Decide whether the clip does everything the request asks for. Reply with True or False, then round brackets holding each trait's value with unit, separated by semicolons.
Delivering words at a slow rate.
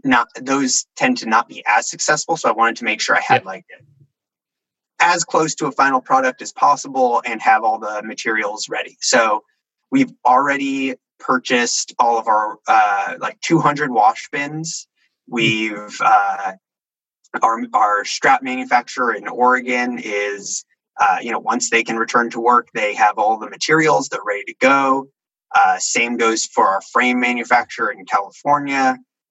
False (165 wpm)